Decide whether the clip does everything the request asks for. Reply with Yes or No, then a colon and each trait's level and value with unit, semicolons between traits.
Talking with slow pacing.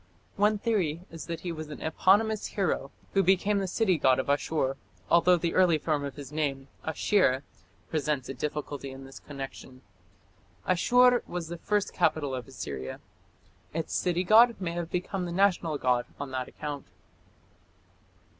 No: average, 160 wpm